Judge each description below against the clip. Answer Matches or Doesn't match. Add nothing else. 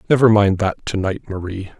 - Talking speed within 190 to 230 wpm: Matches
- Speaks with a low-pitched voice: Matches